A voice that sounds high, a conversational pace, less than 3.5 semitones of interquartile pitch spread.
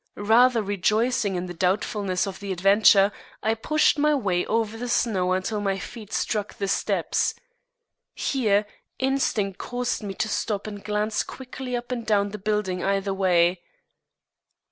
Yes: high, 210 Hz; average, 150 wpm; average, 2.8 semitones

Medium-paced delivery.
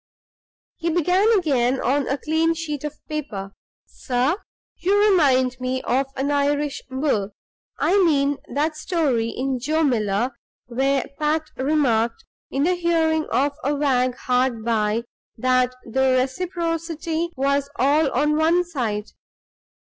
No: slow, 130 wpm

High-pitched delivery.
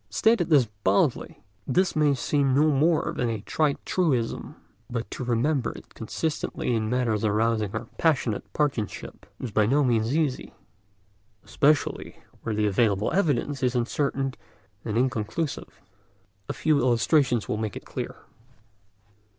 No: low, 125 Hz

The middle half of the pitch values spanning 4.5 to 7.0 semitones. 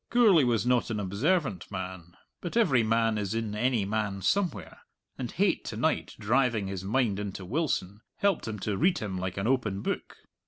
Yes: average, 5.1 semitones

